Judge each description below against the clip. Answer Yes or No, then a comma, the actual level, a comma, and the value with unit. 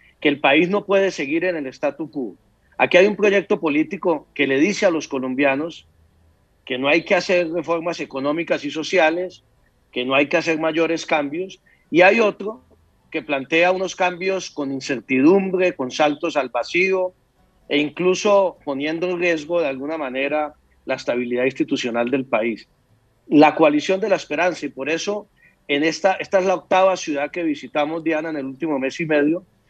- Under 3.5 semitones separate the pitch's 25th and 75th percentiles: No, average, 4.5 semitones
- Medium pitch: Yes, medium, 155 Hz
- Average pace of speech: Yes, average, 175 wpm